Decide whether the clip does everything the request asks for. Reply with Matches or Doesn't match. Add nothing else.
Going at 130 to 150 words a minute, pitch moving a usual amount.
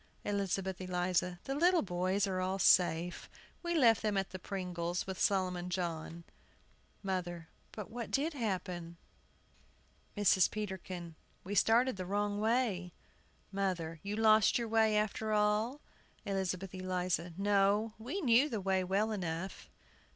Matches